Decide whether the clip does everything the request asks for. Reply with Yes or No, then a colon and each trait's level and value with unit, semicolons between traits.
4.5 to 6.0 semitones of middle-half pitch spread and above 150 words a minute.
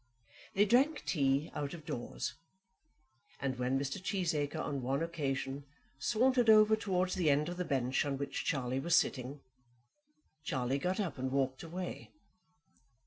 No: wide, 5.4 semitones; average, 145 wpm